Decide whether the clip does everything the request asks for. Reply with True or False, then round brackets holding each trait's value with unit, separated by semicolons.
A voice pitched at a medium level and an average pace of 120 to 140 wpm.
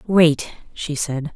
True (155 Hz; 135 wpm)